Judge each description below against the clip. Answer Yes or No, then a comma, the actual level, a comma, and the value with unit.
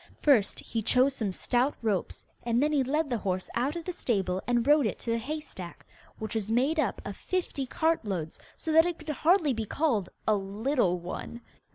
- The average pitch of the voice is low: No, high, 245 Hz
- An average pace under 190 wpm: No, fast, 205 wpm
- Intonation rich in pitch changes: Yes, wide, 6.2 semitones